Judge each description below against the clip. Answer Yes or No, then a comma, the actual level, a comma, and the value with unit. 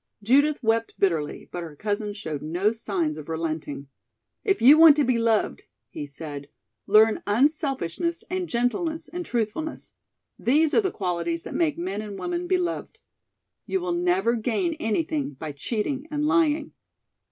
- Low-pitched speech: No, high, 230 Hz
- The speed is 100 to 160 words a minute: Yes, average, 150 wpm